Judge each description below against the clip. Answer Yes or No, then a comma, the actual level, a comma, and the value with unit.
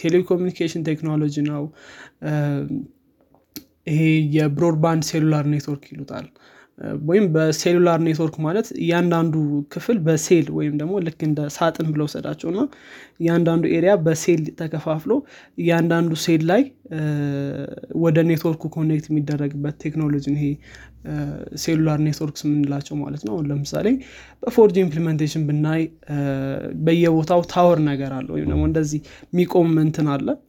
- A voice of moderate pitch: Yes, medium, 155 Hz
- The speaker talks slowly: No, average, 105 wpm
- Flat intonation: Yes, narrow, 2.2 semitones